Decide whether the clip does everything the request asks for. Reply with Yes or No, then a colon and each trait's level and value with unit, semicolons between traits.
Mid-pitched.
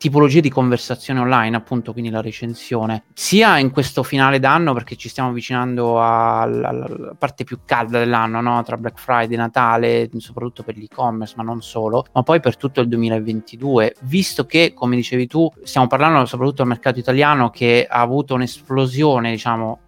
No: low, 125 Hz